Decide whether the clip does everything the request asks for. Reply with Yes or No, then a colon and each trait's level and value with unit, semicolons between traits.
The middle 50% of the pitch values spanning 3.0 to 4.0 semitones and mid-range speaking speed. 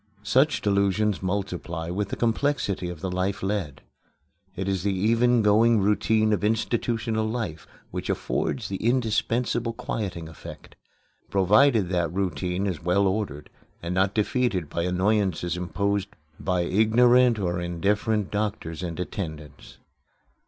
No: average, 3.5 semitones; slow, 130 wpm